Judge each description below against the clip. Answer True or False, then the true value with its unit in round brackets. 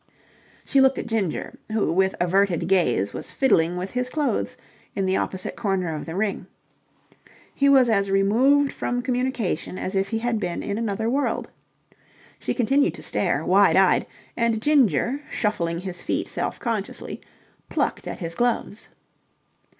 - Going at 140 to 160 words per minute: True (155 wpm)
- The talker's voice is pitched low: False (210 Hz)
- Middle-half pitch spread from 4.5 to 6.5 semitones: True (5.1 semitones)